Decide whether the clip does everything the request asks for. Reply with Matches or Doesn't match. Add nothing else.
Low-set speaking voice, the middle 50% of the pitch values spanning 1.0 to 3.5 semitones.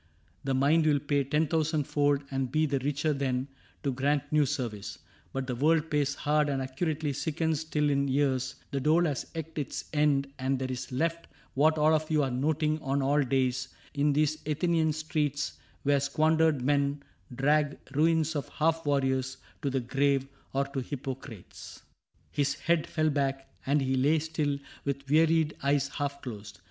Doesn't match